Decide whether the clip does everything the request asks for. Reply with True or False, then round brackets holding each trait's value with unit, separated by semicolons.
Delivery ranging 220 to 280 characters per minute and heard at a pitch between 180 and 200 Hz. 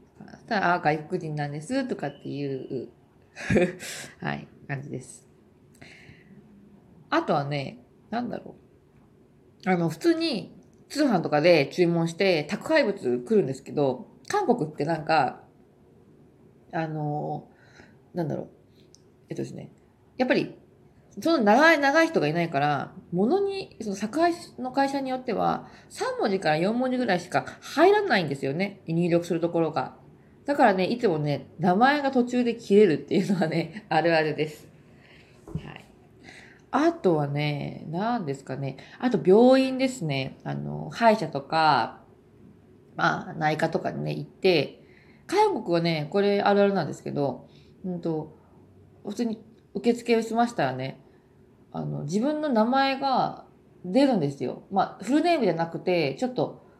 True (270 characters per minute; 185 Hz)